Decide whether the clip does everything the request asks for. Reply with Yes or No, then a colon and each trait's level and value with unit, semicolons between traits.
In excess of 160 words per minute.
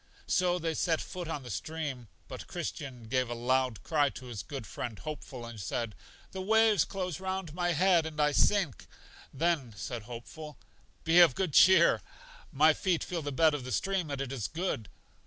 Yes: average, 190 wpm